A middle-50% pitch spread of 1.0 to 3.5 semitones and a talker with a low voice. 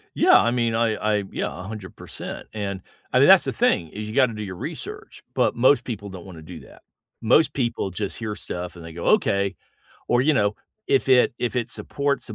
No: average, 4.0 semitones; low, 105 Hz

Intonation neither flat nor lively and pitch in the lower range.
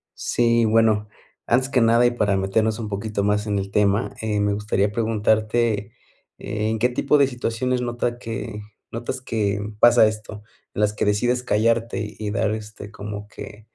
No: narrow, 2.1 semitones; low, 110 Hz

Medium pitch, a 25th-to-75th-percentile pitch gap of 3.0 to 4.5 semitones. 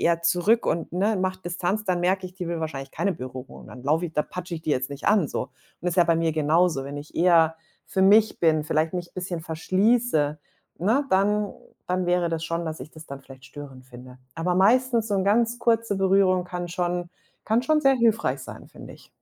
Yes: medium, 175 Hz; average, 3.9 semitones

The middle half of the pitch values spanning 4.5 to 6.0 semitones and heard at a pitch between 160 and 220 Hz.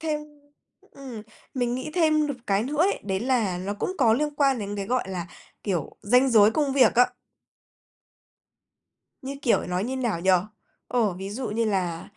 No: average, 5.2 semitones; high, 235 Hz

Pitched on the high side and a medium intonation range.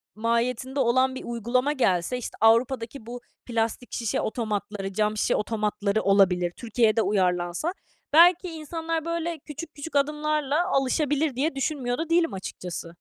No: high, 245 Hz; wide, 5.9 semitones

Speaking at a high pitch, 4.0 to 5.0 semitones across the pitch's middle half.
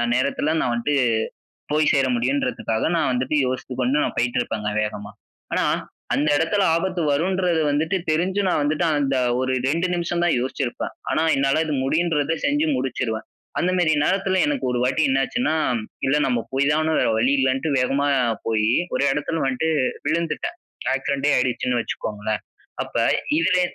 No: medium, 145 Hz; average, 4.6 semitones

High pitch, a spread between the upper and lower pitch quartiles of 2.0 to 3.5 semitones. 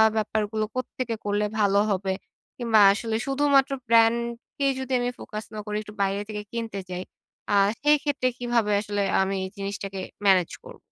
Yes: high, 220 Hz; average, 3.2 semitones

